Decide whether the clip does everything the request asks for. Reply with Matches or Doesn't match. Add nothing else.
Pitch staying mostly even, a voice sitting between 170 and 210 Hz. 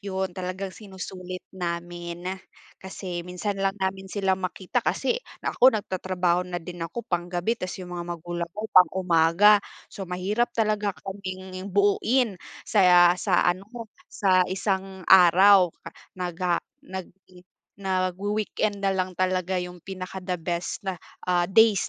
Matches